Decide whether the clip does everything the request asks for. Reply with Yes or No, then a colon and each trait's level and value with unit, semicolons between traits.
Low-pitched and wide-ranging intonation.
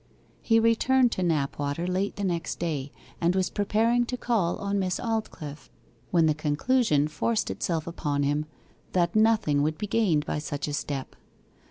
No: medium, 175 Hz; wide, 6.4 semitones